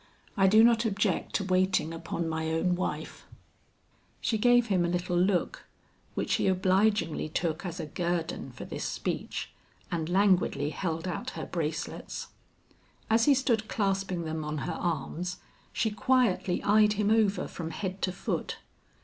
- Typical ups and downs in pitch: Yes, average, 3.9 semitones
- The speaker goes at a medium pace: Yes, average, 155 wpm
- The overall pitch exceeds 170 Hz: Yes, medium, 185 Hz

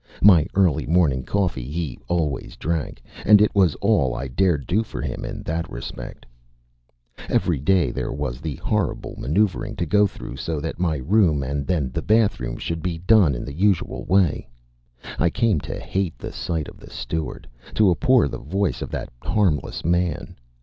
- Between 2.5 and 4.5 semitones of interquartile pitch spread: No, average, 5.2 semitones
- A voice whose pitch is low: Yes, very low, 85 Hz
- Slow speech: No, average, 175 wpm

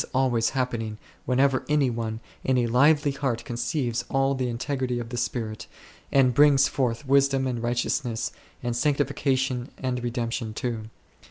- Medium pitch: No, low, 125 Hz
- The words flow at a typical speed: Yes, average, 155 wpm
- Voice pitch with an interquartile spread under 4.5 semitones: Yes, narrow, 2.4 semitones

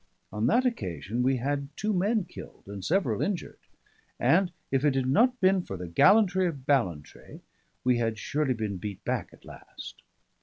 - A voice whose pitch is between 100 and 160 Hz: Yes, low, 135 Hz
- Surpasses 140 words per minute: Yes, average, 175 wpm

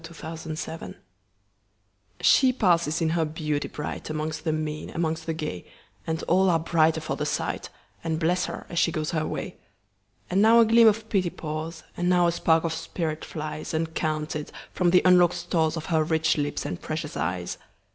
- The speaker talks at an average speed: Yes, average, 165 wpm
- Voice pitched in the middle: Yes, medium, 160 Hz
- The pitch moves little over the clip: Yes, narrow, 1.9 semitones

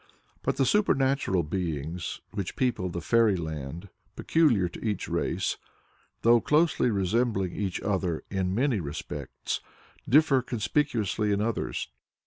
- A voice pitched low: Yes, low, 100 Hz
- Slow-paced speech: Yes, slow, 120 wpm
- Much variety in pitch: Yes, wide, 5.8 semitones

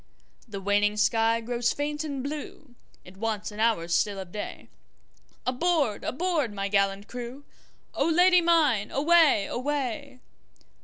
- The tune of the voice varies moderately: No, wide, 6.3 semitones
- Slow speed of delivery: Yes, slow, 115 wpm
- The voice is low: No, high, 235 Hz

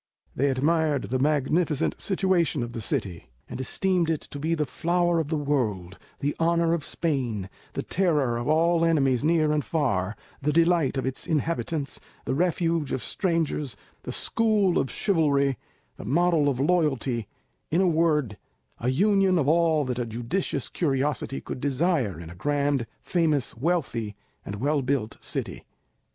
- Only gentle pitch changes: No, average, 4.5 semitones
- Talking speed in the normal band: Yes, average, 160 wpm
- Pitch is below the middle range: No, medium, 150 Hz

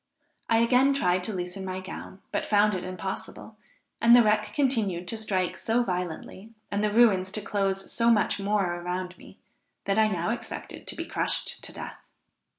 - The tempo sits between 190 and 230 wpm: No, average, 180 wpm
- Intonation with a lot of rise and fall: No, average, 3.3 semitones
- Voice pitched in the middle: No, high, 205 Hz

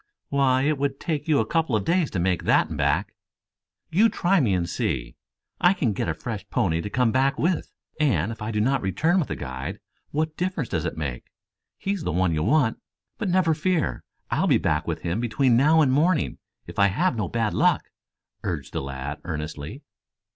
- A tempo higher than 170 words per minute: Yes, fast, 205 wpm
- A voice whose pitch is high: No, low, 125 Hz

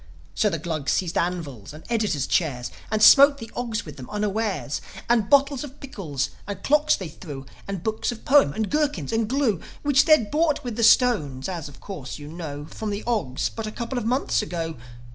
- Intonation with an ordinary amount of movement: No, wide, 7.6 semitones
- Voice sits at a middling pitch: No, high, 210 Hz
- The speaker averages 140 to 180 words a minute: No, average, 200 wpm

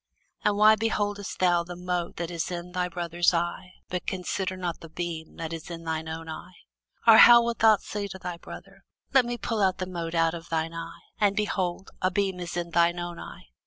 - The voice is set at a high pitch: No, medium, 180 Hz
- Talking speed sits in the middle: No, fast, 220 wpm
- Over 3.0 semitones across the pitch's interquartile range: No, narrow, 2.5 semitones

